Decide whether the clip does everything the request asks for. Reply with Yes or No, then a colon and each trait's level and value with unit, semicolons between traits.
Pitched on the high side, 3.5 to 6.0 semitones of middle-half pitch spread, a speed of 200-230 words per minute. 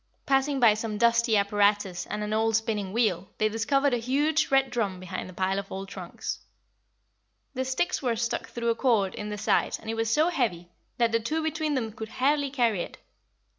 Yes: high, 225 Hz; average, 4.2 semitones; fast, 205 wpm